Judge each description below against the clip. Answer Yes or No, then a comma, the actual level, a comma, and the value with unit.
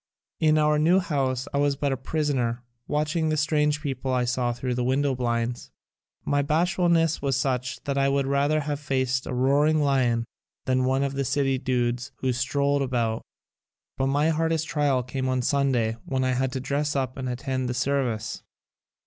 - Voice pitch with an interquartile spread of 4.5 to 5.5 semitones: No, narrow, 2.5 semitones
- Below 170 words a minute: No, average, 185 wpm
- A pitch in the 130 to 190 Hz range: Yes, low, 135 Hz